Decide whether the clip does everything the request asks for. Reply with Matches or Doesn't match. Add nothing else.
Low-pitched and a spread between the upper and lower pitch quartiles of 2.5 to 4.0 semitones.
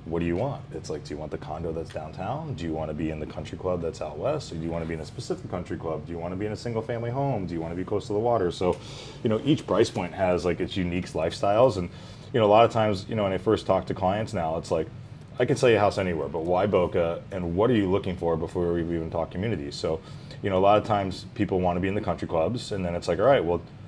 Doesn't match